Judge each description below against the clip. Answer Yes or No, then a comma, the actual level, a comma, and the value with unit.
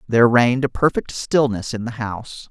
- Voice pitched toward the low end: Yes, low, 120 Hz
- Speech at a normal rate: Yes, average, 190 wpm